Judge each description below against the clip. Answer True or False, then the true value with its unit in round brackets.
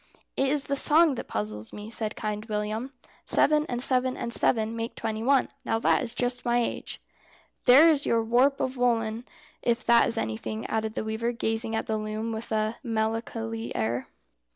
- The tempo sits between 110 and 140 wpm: False (185 wpm)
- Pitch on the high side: True (230 Hz)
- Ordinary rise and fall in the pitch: False (2.2 semitones)